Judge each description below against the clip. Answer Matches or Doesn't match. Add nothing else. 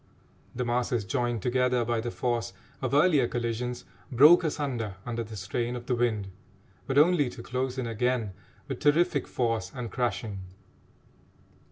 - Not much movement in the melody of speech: Matches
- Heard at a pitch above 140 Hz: Doesn't match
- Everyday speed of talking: Matches